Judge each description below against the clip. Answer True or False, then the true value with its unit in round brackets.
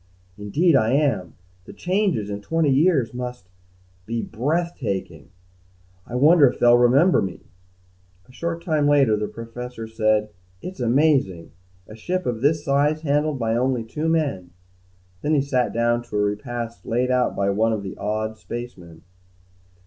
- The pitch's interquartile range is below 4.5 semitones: False (5.2 semitones)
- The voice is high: False (125 Hz)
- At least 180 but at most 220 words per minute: False (155 wpm)